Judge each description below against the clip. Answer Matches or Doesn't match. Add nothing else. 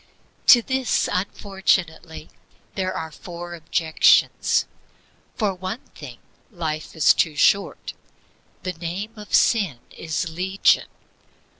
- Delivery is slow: Matches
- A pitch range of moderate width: Matches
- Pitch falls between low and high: Matches